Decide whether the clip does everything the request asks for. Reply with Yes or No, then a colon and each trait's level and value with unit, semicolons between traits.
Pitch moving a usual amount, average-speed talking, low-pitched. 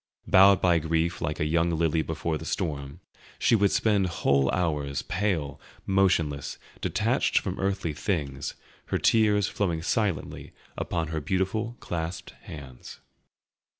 No: average, 4.3 semitones; slow, 130 wpm; very low, 85 Hz